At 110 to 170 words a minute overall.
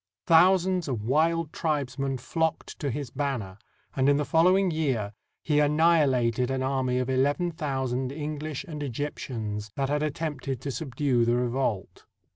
Yes: average, 155 wpm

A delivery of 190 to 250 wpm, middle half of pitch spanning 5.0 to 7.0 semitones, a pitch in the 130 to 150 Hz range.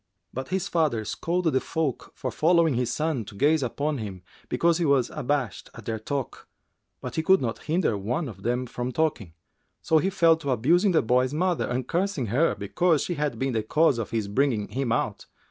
Yes: fast, 205 wpm; wide, 5.4 semitones; medium, 140 Hz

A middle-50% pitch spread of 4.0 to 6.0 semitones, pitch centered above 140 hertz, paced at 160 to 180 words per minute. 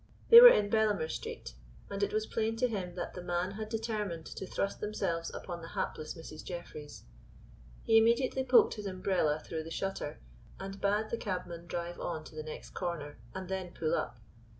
No: average, 4.3 semitones; medium, 185 Hz; average, 190 wpm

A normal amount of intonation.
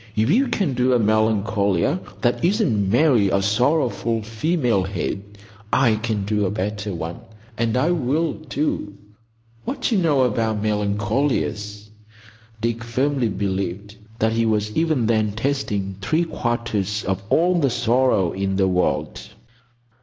Yes: average, 4.3 semitones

